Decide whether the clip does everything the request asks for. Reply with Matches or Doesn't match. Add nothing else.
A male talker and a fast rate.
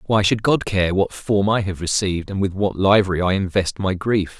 Matches